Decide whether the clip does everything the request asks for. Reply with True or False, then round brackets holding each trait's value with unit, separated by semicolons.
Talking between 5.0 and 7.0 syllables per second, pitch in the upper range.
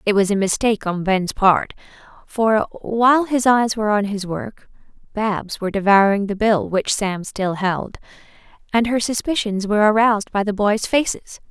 False (4.8 syllables/s; 210 Hz)